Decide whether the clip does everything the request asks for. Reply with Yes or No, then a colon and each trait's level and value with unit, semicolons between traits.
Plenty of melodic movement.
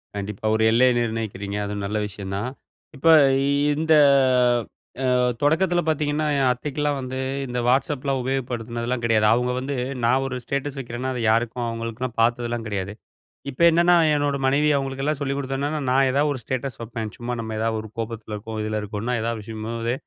No: average, 3.4 semitones